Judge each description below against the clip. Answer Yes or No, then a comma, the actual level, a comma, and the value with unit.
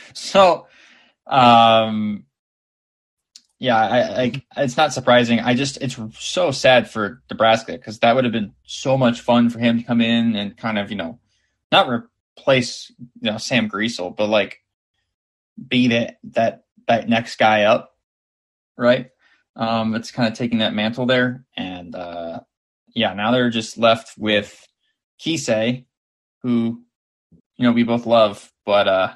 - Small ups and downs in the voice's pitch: Yes, narrow, 2.2 semitones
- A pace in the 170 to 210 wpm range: No, average, 150 wpm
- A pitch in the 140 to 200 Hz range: No, low, 115 Hz